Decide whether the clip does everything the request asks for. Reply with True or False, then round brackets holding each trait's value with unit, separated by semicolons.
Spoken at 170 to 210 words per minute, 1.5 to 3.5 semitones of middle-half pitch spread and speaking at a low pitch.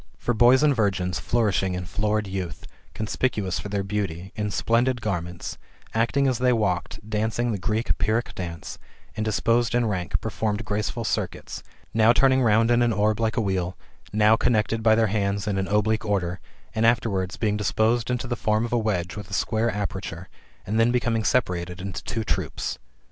True (180 wpm; 3.0 semitones; 110 Hz)